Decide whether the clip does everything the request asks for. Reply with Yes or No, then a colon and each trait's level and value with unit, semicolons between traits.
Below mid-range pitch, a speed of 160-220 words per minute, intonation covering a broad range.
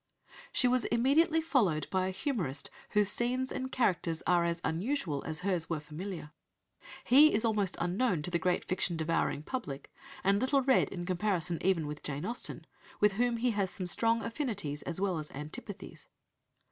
No: high, 190 Hz; average, 170 wpm; wide, 6.2 semitones